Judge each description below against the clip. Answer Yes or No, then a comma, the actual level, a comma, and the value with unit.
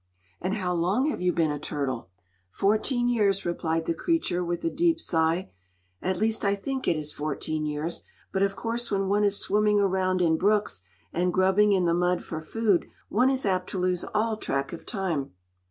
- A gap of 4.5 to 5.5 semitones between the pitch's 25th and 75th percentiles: No, average, 3.9 semitones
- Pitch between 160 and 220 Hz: Yes, medium, 185 Hz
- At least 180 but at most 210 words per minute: Yes, average, 195 wpm